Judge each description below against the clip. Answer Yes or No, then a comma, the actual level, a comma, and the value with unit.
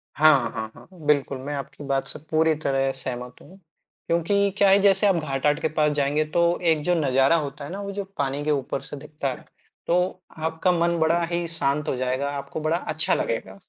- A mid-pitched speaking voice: Yes, medium, 150 Hz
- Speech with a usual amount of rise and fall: Yes, average, 3.7 semitones